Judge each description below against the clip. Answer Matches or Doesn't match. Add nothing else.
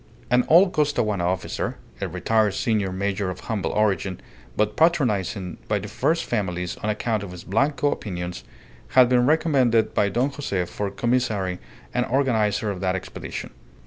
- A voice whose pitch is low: Matches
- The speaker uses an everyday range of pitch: Matches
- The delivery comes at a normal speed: Matches